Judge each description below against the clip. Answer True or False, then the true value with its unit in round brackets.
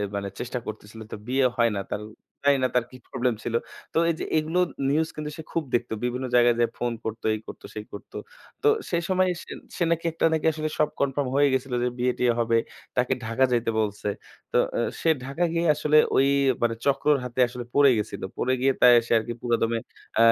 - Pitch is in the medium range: False (125 Hz)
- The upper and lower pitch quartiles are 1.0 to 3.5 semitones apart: False (4.1 semitones)